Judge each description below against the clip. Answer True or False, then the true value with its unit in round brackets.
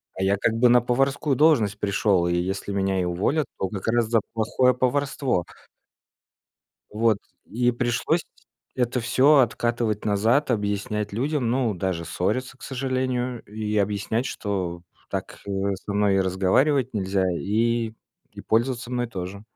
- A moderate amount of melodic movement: True (4.0 semitones)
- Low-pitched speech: True (110 Hz)